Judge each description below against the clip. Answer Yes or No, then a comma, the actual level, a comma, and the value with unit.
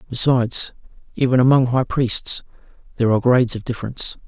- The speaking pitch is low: Yes, low, 125 Hz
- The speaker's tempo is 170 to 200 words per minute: No, average, 140 wpm